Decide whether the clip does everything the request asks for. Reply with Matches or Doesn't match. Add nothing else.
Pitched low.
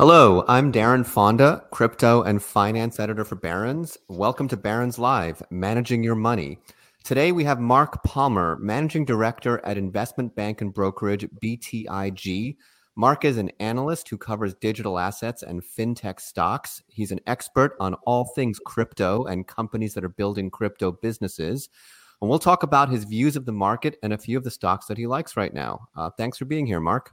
Matches